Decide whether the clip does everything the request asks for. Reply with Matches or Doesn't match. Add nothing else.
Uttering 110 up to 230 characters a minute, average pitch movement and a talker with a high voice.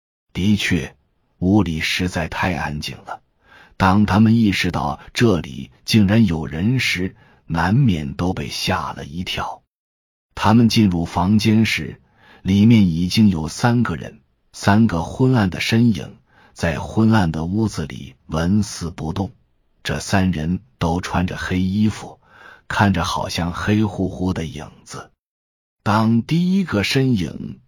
Doesn't match